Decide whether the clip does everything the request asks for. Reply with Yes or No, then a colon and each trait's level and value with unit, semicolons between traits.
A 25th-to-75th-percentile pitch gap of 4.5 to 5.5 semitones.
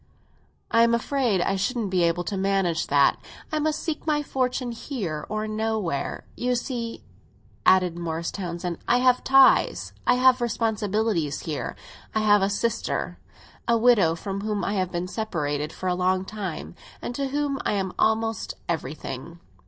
Yes: average, 5.1 semitones